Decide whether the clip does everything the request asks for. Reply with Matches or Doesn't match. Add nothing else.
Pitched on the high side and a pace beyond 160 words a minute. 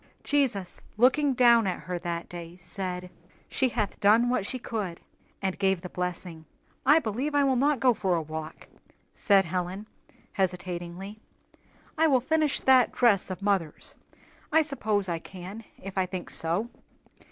Doesn't match